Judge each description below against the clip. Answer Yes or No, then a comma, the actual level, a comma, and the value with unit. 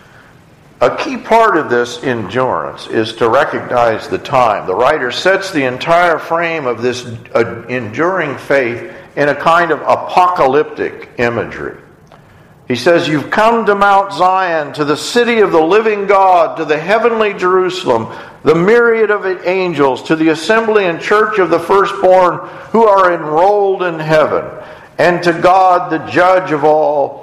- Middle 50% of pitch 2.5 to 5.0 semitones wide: Yes, average, 4.6 semitones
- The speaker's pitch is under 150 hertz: No, medium, 180 Hz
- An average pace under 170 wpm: Yes, average, 150 wpm